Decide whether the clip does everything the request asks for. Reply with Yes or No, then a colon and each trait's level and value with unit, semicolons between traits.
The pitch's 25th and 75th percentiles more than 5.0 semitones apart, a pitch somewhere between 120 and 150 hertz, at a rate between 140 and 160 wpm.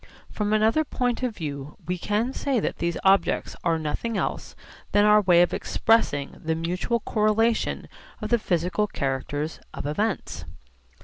No: wide, 5.6 semitones; high, 200 Hz; average, 150 wpm